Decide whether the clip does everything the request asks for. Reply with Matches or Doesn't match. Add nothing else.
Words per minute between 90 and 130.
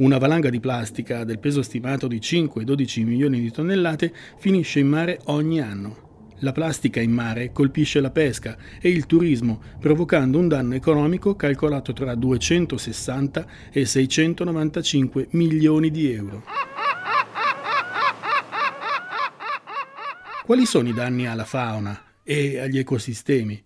Matches